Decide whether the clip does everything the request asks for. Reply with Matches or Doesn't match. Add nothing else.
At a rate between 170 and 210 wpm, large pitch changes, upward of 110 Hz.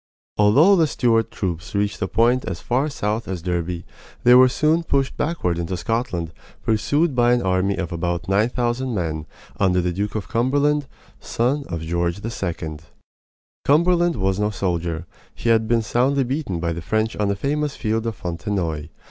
Doesn't match